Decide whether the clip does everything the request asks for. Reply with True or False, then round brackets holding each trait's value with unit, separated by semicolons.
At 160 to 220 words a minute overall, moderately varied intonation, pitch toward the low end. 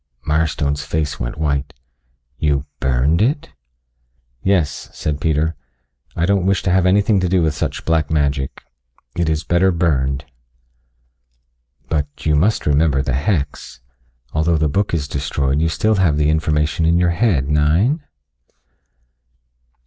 False (140 wpm; 3.3 semitones; 80 Hz)